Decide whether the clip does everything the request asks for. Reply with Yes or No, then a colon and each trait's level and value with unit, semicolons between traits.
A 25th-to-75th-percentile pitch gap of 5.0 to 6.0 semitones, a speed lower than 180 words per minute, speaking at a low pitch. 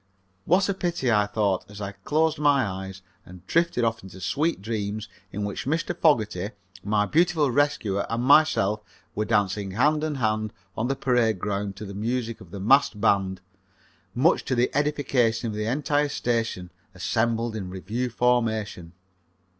Yes: wide, 5.5 semitones; average, 160 wpm; low, 115 Hz